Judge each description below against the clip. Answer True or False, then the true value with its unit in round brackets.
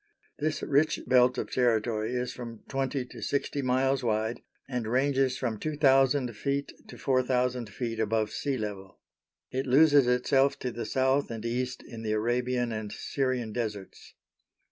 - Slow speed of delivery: False (150 wpm)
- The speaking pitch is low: True (125 Hz)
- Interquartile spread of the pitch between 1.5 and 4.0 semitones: True (2.8 semitones)